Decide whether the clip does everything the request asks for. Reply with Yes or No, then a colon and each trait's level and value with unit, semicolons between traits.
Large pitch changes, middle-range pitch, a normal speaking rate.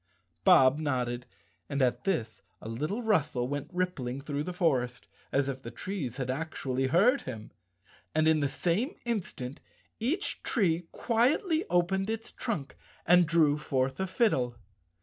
Yes: wide, 6.6 semitones; medium, 155 Hz; average, 150 wpm